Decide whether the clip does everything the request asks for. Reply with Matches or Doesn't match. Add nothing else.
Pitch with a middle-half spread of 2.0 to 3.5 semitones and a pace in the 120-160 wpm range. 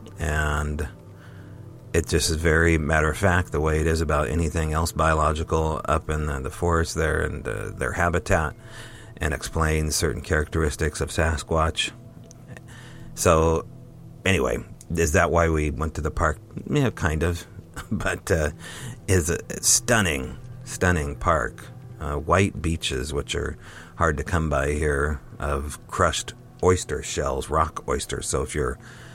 Doesn't match